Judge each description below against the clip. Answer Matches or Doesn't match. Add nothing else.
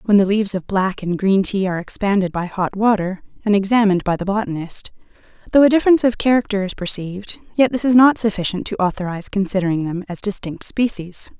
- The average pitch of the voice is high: Matches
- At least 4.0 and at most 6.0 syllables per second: Doesn't match